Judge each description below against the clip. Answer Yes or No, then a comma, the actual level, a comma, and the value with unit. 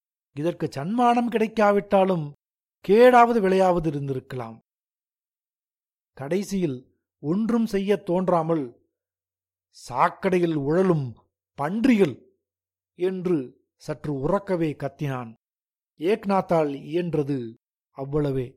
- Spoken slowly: Yes, slow, 65 wpm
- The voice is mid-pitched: Yes, medium, 165 Hz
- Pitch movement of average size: No, wide, 5.9 semitones